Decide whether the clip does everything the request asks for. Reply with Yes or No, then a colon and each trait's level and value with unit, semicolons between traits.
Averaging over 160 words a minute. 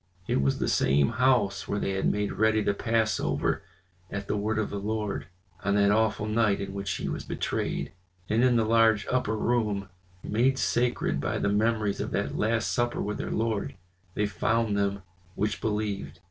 Yes: average, 185 wpm